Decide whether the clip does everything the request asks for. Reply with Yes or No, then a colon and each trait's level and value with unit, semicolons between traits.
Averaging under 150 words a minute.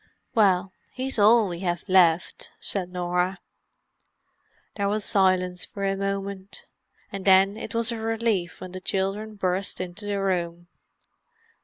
Yes: average, 140 wpm